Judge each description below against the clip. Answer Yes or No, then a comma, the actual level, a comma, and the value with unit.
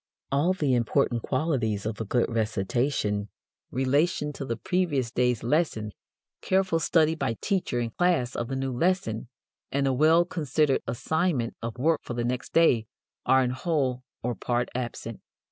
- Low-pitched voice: Yes, low, 130 Hz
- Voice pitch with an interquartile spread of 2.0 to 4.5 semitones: No, average, 5.1 semitones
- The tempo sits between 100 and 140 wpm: No, average, 160 wpm